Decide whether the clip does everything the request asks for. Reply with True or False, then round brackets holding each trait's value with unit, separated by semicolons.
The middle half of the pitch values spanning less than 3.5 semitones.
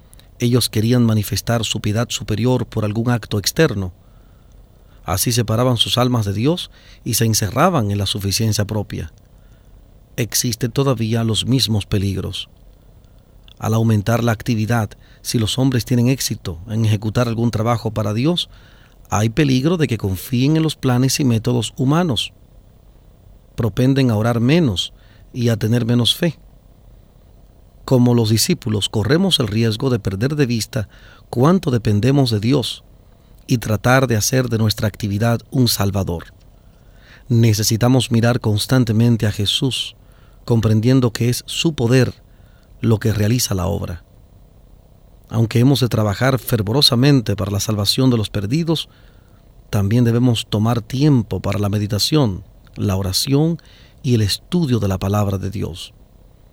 True (3.1 semitones)